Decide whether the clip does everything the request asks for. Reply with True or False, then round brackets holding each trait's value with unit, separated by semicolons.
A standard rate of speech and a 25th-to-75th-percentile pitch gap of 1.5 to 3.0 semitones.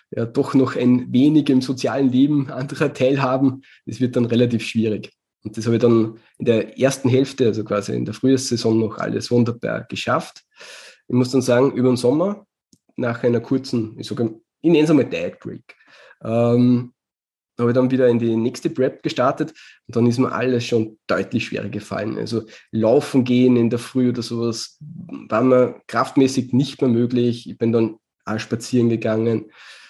True (175 wpm; 2.4 semitones)